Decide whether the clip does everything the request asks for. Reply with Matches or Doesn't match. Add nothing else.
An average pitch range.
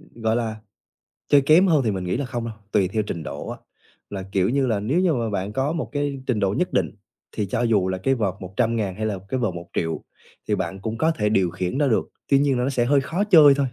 Doesn't match